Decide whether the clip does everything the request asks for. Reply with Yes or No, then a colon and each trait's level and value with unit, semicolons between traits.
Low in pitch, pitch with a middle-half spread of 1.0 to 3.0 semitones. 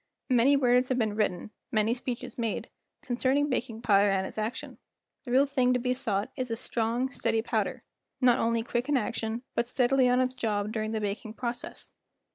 No: high, 240 Hz; narrow, 2.4 semitones